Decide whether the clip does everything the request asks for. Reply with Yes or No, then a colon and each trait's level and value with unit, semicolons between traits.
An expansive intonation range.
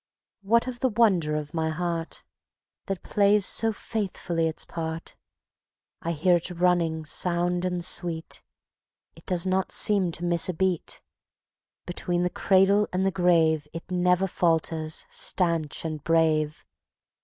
No: narrow, 2.6 semitones